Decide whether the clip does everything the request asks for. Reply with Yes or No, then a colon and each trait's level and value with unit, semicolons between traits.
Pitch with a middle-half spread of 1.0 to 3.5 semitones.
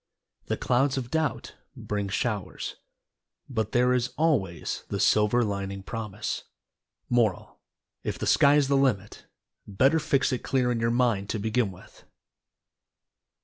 No: average, 4.3 semitones